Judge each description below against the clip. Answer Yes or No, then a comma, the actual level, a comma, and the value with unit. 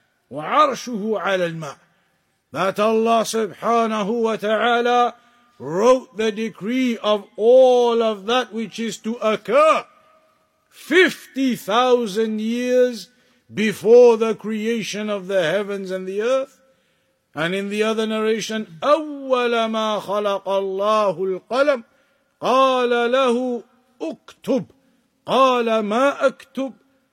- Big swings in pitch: No, average, 3.1 semitones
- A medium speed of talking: No, slow, 100 wpm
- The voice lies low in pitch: No, high, 230 Hz